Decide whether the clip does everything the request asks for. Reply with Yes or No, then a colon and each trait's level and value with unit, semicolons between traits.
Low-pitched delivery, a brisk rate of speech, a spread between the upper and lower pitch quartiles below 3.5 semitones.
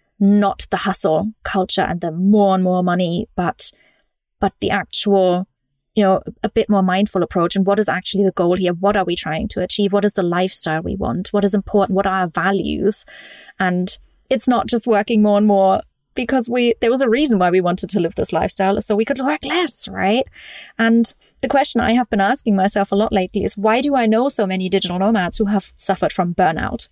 No: high, 200 Hz; fast, 220 wpm; average, 3.0 semitones